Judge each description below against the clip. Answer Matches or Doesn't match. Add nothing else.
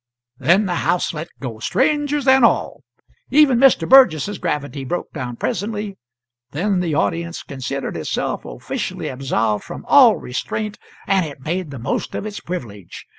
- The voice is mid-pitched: Matches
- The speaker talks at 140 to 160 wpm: Matches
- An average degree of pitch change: Doesn't match